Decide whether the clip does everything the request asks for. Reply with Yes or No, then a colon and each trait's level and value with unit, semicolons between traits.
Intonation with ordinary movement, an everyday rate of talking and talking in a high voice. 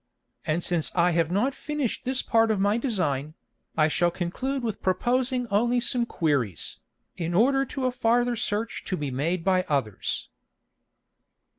No: wide, 6.7 semitones; average, 155 wpm; high, 200 Hz